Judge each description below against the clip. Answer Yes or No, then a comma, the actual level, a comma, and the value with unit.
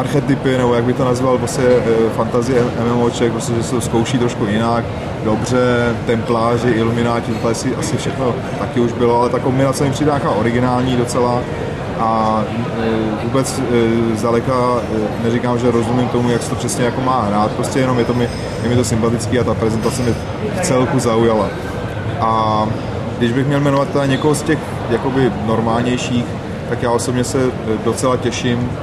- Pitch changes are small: Yes, narrow, 1.6 semitones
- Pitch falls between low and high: No, low, 120 Hz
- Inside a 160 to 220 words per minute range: Yes, average, 165 wpm